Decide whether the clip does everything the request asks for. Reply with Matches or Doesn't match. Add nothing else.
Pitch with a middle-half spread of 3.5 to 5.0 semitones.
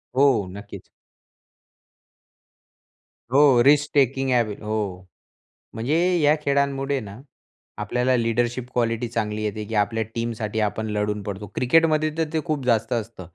Matches